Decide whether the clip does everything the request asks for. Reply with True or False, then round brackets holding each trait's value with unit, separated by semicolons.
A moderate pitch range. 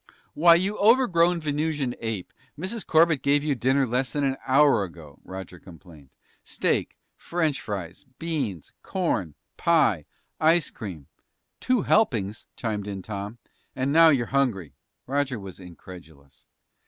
False (8.9 semitones)